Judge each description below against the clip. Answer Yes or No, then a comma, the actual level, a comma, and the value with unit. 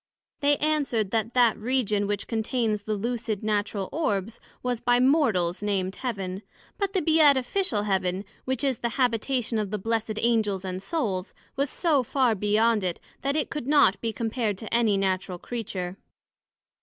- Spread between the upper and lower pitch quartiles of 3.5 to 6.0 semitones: Yes, average, 4.2 semitones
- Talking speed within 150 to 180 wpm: Yes, average, 160 wpm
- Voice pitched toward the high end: Yes, high, 225 Hz